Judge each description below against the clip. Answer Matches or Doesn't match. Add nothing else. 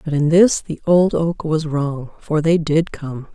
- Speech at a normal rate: Doesn't match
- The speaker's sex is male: Doesn't match